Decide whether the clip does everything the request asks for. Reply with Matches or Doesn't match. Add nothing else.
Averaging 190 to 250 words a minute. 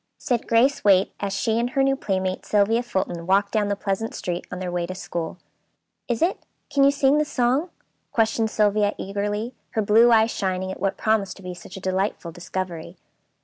Matches